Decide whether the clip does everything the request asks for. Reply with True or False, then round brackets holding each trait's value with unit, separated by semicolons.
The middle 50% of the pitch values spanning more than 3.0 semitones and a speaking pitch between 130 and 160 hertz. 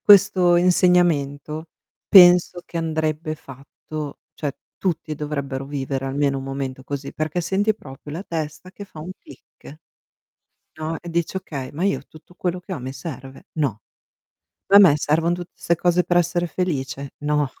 True (3.9 semitones; 155 Hz)